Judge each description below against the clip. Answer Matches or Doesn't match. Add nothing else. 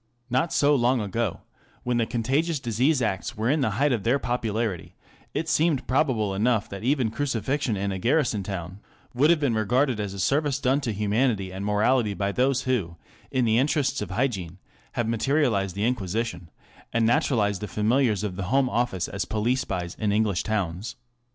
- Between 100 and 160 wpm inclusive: Doesn't match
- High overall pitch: Doesn't match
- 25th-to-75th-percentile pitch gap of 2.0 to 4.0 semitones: Doesn't match